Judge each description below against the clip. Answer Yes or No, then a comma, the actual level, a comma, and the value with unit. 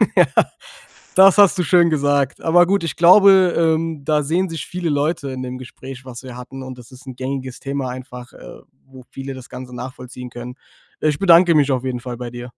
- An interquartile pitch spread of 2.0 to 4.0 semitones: No, average, 4.6 semitones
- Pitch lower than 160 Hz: Yes, low, 135 Hz